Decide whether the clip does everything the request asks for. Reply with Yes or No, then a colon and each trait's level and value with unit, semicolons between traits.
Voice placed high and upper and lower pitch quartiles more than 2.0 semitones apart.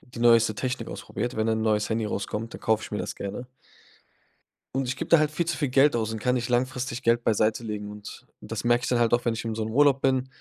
No: low, 120 Hz; average, 2.7 semitones